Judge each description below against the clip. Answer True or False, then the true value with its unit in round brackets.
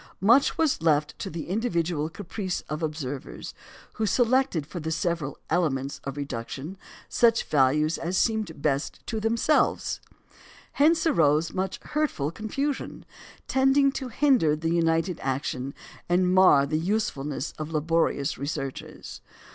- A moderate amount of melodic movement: False (6.8 semitones)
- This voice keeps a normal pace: False (125 wpm)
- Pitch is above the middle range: False (165 Hz)